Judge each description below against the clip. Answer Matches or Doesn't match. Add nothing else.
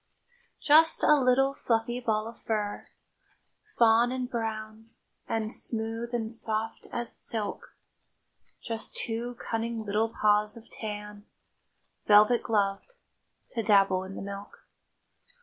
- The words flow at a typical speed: Doesn't match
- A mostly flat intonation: Matches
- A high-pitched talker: Matches